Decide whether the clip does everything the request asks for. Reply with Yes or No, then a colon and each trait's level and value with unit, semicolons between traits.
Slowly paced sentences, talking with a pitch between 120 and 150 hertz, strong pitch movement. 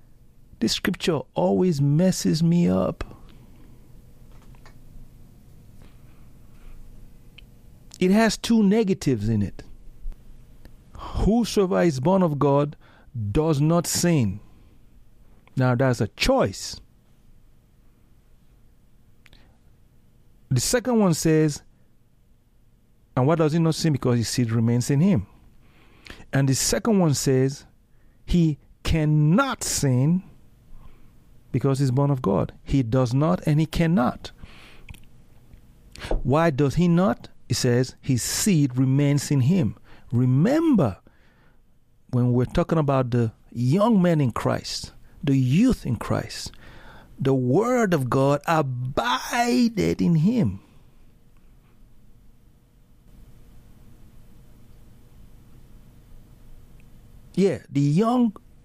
Yes: slow, 95 wpm; low, 135 Hz; wide, 6.1 semitones